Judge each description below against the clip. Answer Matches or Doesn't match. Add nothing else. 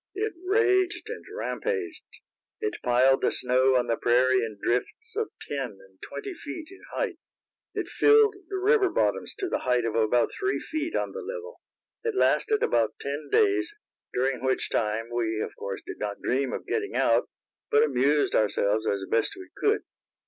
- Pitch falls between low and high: Matches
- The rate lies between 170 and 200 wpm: Matches